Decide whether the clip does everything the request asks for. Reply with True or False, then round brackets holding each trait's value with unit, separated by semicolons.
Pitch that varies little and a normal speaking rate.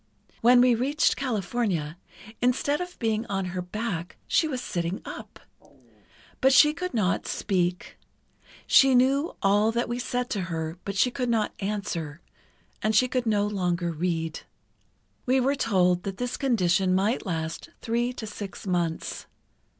False (5.6 semitones; 150 wpm)